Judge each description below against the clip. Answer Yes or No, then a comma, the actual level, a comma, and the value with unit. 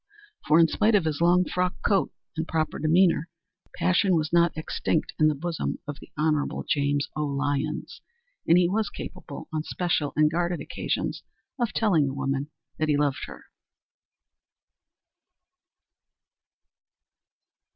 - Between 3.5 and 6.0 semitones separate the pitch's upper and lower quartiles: No, average, 3.0 semitones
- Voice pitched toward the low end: No, medium, 160 Hz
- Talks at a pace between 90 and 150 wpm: Yes, average, 140 wpm